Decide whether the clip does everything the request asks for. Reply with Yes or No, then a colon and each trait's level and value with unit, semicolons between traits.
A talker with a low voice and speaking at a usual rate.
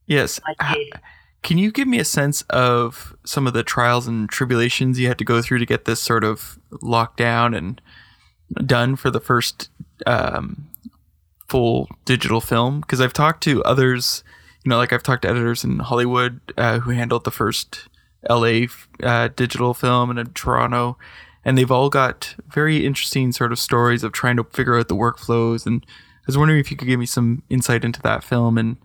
Yes: low, 120 Hz; average, 190 wpm